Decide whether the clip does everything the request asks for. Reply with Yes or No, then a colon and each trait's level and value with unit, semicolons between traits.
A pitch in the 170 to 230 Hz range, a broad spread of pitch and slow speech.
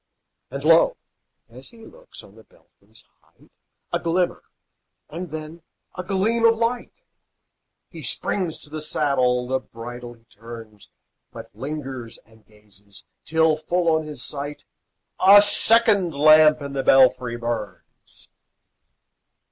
No: medium, 150 Hz; wide, 6.3 semitones; slow, 130 wpm